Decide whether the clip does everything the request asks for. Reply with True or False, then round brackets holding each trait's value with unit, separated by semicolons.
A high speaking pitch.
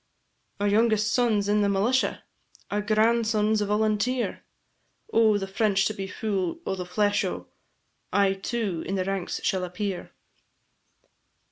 True (205 Hz)